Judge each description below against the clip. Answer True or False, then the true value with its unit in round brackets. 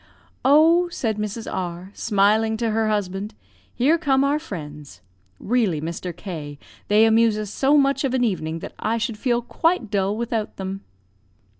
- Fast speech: False (160 wpm)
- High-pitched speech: True (220 Hz)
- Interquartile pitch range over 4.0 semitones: True (4.5 semitones)